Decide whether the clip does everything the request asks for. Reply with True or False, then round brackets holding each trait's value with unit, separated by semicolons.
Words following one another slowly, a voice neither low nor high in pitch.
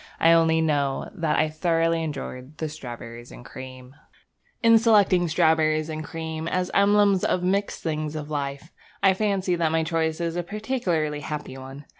False (160 wpm; 160 Hz)